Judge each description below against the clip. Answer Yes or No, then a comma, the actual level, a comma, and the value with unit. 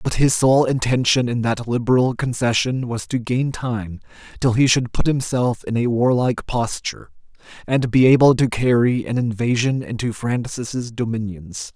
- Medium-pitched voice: No, low, 120 Hz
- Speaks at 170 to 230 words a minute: No, average, 160 wpm